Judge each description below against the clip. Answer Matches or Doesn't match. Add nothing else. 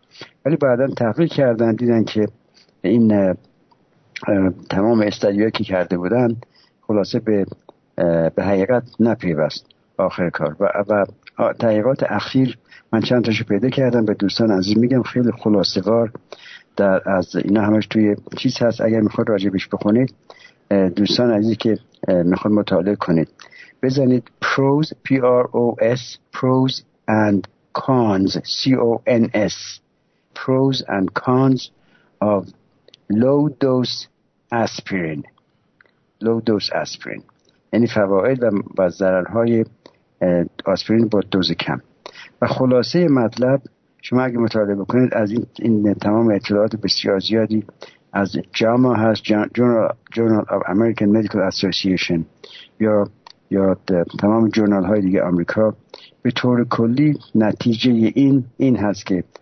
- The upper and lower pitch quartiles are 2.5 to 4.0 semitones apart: Matches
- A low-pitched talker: Matches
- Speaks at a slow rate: Matches